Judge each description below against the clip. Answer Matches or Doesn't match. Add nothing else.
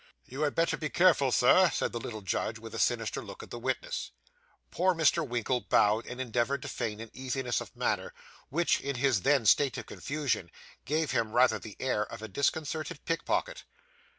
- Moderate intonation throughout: Matches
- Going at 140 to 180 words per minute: Doesn't match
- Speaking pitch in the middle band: Doesn't match